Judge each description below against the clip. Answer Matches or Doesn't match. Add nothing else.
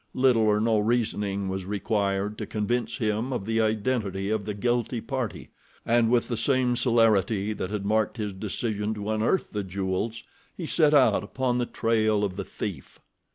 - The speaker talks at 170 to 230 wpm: Matches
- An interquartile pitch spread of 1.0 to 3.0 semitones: Matches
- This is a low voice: Matches